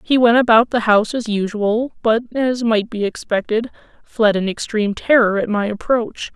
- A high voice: Yes, high, 225 Hz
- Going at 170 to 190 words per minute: Yes, average, 180 wpm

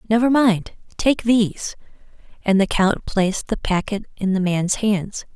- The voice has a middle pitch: No, high, 205 Hz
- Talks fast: No, average, 145 wpm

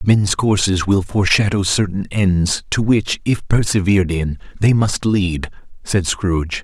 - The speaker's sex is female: No, male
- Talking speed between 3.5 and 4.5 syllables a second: Yes, 4.2 syllables/s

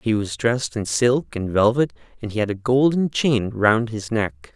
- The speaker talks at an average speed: No, fast, 210 wpm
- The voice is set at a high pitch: No, low, 115 Hz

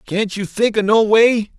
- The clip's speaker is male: Yes, male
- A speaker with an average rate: No, fast, 230 wpm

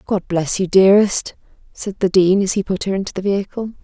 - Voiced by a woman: Yes, female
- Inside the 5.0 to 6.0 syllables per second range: Yes, 5.8 syllables/s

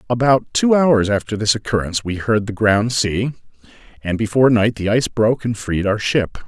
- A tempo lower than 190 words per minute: No, average, 195 wpm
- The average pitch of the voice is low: Yes, low, 110 Hz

